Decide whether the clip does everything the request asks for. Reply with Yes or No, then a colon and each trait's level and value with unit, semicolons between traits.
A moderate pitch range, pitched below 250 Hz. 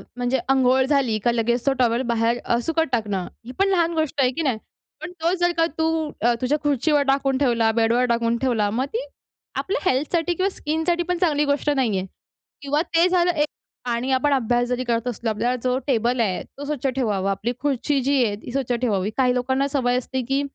No: average, 3.8 semitones; very high, 260 Hz